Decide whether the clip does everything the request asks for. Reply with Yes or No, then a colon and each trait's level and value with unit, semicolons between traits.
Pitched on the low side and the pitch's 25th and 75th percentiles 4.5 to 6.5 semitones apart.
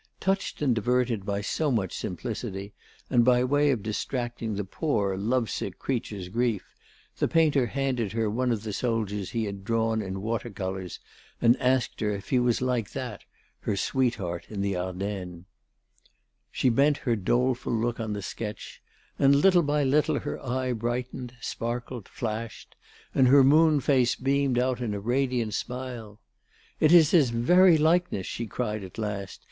No: low, 120 Hz; average, 4.0 semitones